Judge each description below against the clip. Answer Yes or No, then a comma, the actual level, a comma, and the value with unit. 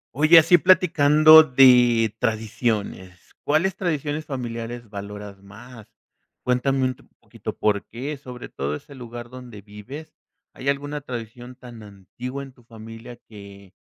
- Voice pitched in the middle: No, low, 125 Hz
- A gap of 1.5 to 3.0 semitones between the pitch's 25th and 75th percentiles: No, average, 4.3 semitones